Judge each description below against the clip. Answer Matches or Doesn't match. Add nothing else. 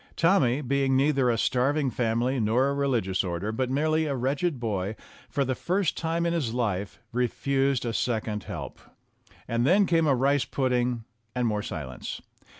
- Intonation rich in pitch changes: Doesn't match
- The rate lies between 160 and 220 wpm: Matches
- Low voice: Matches